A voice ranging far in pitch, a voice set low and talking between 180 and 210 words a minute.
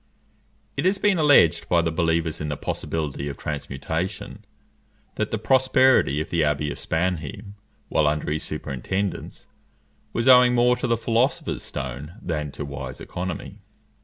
No: wide, 7.7 semitones; very low, 85 Hz; average, 150 wpm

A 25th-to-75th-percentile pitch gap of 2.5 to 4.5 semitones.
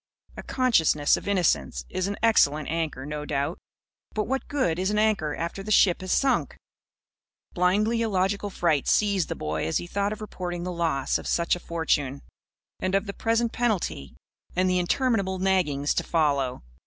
No: average, 5.2 semitones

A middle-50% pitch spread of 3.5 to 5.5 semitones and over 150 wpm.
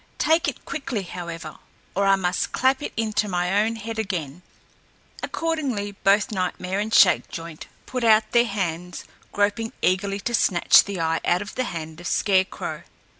Yes: average, 4.0 semitones; average, 160 wpm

